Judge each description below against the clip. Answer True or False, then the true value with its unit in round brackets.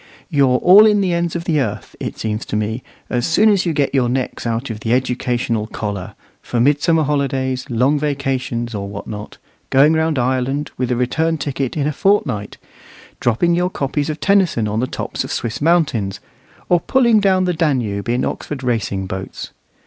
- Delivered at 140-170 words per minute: False (185 wpm)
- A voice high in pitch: False (135 Hz)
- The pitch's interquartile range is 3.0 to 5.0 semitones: False (5.5 semitones)